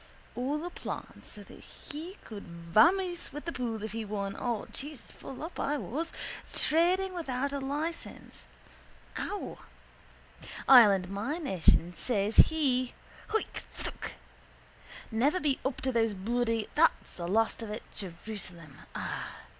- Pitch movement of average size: No, wide, 6.6 semitones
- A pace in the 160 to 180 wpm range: No, slow, 135 wpm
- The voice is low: No, very high, 250 Hz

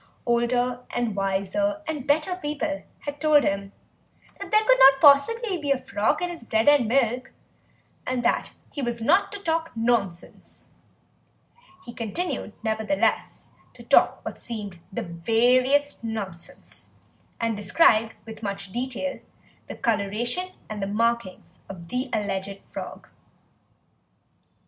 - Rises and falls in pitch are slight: No, average, 5.3 semitones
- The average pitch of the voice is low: No, high, 240 Hz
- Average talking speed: No, slow, 130 wpm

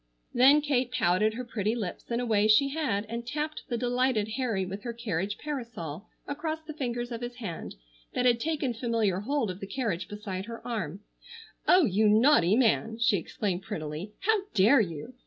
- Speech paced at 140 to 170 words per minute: No, average, 185 wpm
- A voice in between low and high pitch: No, high, 230 Hz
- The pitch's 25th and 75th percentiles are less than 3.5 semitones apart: No, average, 4.0 semitones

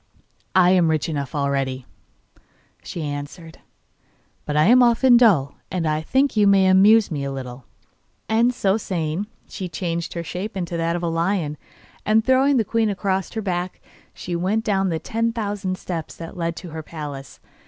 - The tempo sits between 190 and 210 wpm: No, average, 175 wpm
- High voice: No, medium, 180 Hz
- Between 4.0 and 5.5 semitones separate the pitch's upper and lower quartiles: Yes, average, 4.8 semitones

